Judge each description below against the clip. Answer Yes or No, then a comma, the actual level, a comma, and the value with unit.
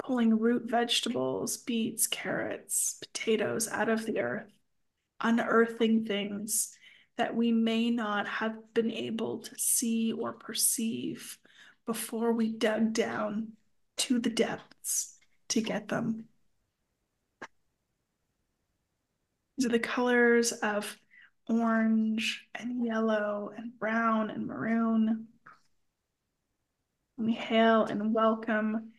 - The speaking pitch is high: Yes, high, 225 Hz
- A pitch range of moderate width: No, narrow, 1.0 semitones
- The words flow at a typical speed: No, slow, 100 wpm